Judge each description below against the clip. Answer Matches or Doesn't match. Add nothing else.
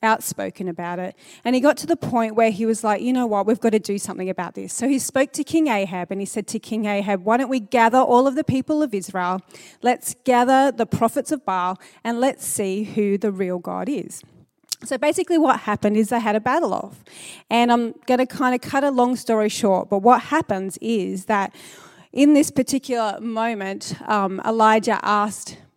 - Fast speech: Matches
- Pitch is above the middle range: Matches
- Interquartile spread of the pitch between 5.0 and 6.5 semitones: Doesn't match